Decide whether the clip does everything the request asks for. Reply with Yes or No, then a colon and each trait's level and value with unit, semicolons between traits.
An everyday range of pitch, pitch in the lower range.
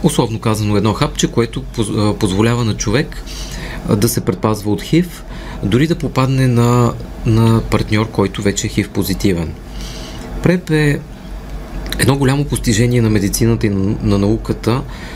Yes: average, 4.2 semitones; low, 110 Hz